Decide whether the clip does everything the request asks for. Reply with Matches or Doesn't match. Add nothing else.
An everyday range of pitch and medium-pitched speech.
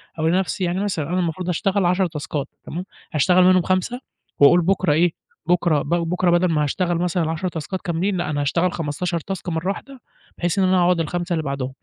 Doesn't match